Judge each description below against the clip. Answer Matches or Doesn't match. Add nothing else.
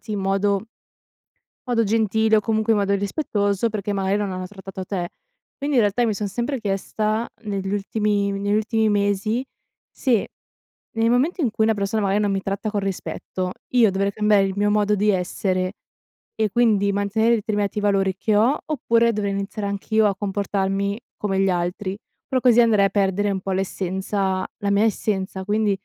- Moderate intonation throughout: Doesn't match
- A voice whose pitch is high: Matches